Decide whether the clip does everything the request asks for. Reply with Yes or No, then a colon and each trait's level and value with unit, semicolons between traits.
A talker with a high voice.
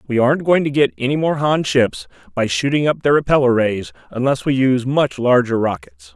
No: low, 125 Hz